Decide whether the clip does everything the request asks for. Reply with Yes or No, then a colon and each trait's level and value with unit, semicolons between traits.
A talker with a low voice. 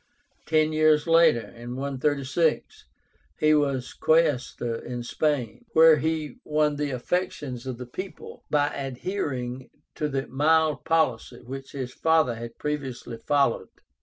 No: medium, 145 Hz